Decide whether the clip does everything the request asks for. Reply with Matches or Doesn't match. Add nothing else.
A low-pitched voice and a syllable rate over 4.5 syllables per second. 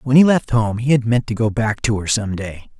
Matches